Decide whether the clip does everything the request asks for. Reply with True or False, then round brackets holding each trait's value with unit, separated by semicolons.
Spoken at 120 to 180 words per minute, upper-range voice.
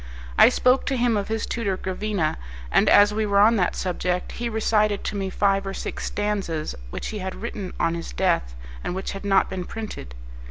False (205 wpm; 200 Hz)